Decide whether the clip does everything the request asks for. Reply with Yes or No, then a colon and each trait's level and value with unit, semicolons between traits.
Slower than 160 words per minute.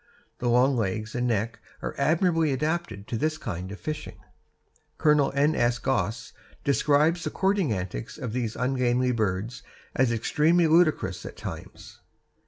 Yes: average, 145 wpm